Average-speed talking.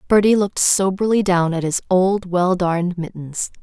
Yes: average, 165 wpm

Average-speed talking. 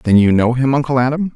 No: fast, 265 wpm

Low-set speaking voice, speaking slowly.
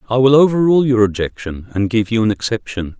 No: low, 115 Hz; average, 200 wpm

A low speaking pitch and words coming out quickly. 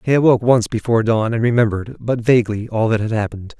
Yes: low, 115 Hz; fast, 215 wpm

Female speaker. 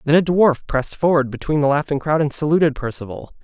No: male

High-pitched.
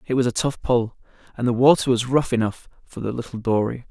No: low, 120 Hz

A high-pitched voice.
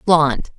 No: medium, 160 Hz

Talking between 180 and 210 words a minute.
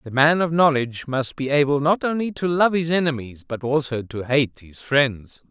Yes: fast, 205 wpm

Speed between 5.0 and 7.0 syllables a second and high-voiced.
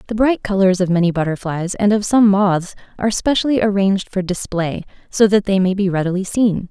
Yes: 5.6 syllables/s; high, 195 Hz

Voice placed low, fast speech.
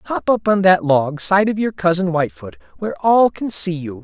No: medium, 175 Hz; fast, 225 wpm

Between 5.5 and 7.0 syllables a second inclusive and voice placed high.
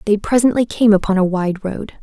Yes: 5.6 syllables/s; high, 205 Hz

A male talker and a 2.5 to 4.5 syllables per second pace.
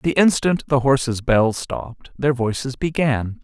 Yes: male; 4.3 syllables/s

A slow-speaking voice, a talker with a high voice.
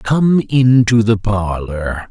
No: slow, 115 wpm; low, 110 Hz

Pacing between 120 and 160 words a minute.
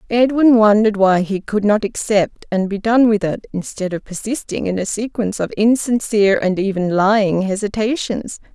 No: average, 170 wpm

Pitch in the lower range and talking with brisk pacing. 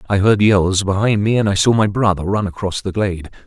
Yes: low, 100 Hz; fast, 240 wpm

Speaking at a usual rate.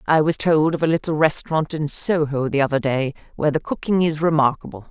No: fast, 210 wpm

